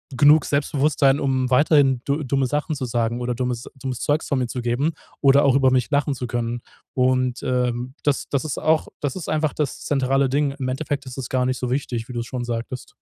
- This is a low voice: Yes, low, 130 Hz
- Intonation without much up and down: Yes, narrow, 2.3 semitones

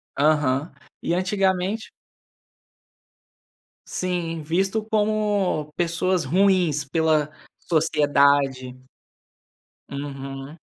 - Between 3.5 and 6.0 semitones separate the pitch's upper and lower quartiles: Yes, average, 4.6 semitones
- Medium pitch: Yes, medium, 165 Hz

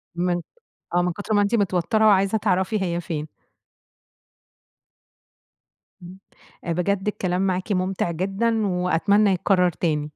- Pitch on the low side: No, medium, 185 Hz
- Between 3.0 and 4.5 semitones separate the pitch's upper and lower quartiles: No, narrow, 2.4 semitones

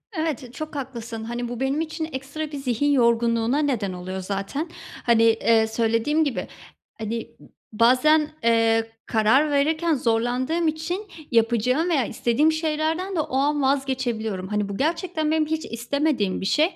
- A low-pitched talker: No, very high, 260 Hz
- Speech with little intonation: No, average, 5.3 semitones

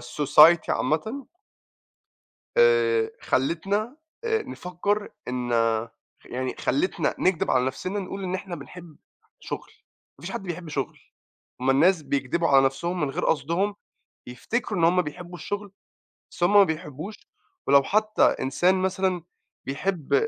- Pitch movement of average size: No, wide, 5.8 semitones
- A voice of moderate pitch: Yes, medium, 175 Hz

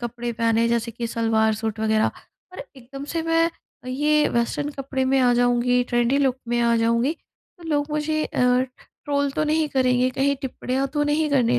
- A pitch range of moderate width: Yes, average, 3.8 semitones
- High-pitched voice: Yes, very high, 255 Hz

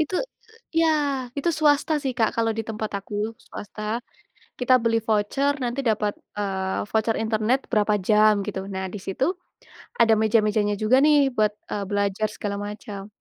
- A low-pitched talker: No, high, 215 Hz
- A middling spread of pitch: No, narrow, 2.2 semitones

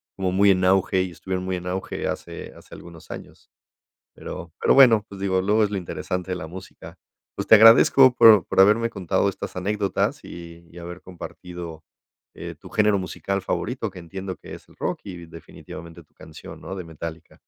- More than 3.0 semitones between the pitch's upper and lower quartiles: No, average, 2.7 semitones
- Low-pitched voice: Yes, very low, 95 Hz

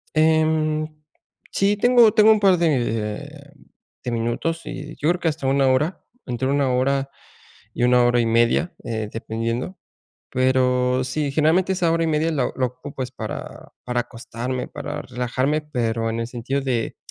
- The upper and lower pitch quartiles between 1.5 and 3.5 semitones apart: No, average, 4.2 semitones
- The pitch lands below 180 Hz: Yes, low, 135 Hz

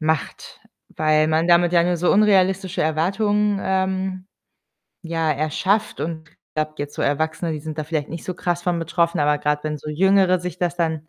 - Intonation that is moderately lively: Yes, average, 3.2 semitones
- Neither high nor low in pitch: Yes, medium, 170 Hz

